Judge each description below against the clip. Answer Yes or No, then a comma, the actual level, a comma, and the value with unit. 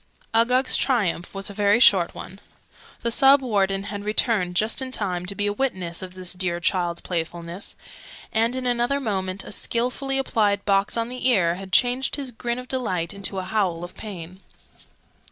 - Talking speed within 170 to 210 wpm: Yes, average, 180 wpm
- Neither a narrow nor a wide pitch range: Yes, average, 4.7 semitones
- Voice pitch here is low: No, high, 205 Hz